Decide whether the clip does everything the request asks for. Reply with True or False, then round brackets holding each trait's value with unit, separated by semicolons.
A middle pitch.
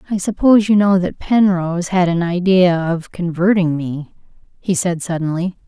True (180 Hz)